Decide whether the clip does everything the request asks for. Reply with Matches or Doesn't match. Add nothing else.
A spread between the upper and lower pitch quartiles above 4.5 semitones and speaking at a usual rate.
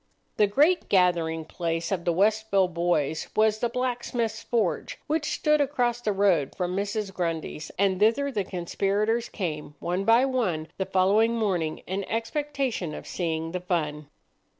Matches